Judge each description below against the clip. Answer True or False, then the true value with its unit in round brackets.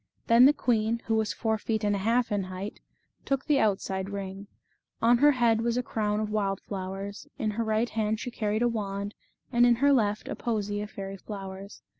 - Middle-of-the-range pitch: False (215 Hz)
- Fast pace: True (210 wpm)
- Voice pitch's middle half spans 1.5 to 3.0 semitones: True (2.6 semitones)